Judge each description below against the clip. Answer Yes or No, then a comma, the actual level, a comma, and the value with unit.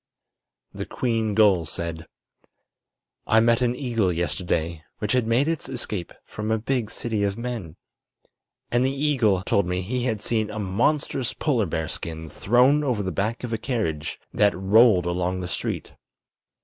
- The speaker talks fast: No, average, 160 wpm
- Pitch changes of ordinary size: Yes, average, 4.9 semitones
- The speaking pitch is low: Yes, low, 110 Hz